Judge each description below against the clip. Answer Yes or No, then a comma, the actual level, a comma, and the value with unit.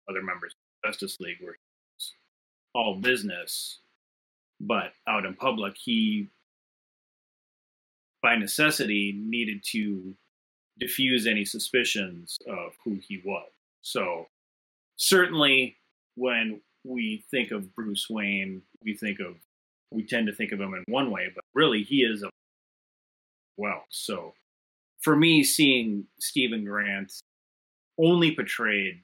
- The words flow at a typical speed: No, slow, 120 wpm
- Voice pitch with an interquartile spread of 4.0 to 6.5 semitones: Yes, average, 5.1 semitones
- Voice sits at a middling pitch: No, low, 110 Hz